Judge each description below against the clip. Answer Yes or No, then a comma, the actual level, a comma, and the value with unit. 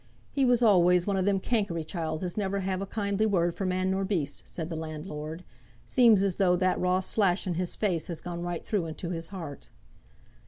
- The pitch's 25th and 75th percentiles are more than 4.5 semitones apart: No, average, 2.8 semitones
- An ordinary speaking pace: No, fast, 210 wpm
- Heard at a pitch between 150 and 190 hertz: Yes, medium, 185 Hz